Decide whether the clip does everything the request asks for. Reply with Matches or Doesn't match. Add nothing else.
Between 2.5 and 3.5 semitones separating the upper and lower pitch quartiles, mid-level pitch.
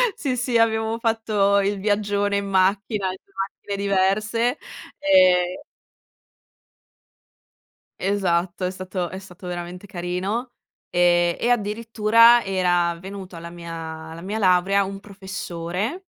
Doesn't match